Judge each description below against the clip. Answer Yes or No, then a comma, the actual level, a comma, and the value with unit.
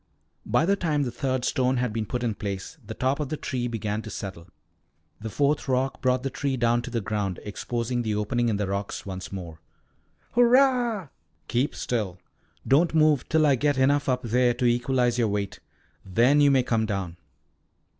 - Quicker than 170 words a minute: Yes, average, 190 wpm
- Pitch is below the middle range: Yes, low, 120 Hz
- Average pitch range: Yes, average, 4.4 semitones